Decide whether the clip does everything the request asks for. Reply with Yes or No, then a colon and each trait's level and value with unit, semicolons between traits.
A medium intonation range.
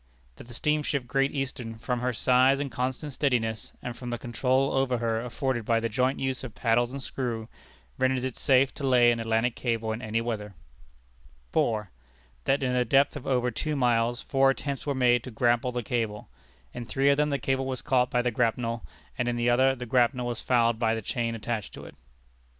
No: narrow, 2.3 semitones